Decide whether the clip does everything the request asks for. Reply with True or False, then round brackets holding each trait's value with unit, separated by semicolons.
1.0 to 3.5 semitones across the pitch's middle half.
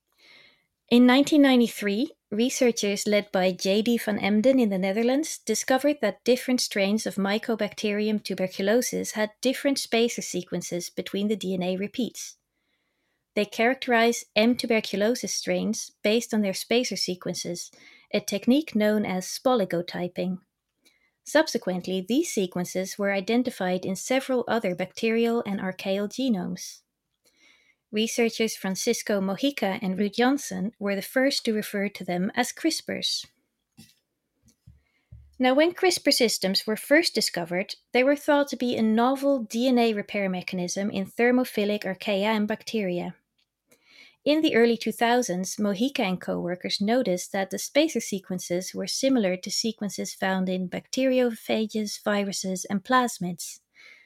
False (4.3 semitones)